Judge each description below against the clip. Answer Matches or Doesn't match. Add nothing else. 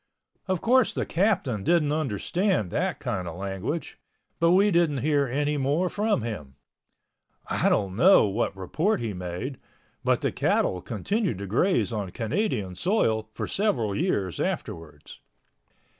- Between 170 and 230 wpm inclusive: Doesn't match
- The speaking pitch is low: Matches